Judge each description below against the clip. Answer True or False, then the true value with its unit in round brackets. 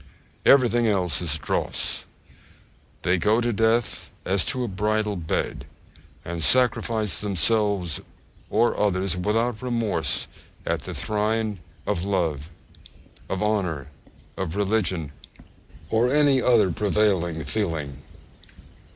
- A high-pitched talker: False (105 Hz)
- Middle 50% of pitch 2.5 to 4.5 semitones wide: True (4.0 semitones)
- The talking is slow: True (110 wpm)